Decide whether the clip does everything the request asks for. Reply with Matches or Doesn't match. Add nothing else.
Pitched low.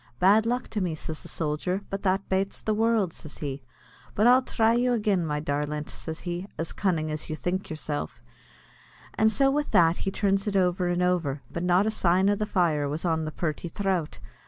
Doesn't match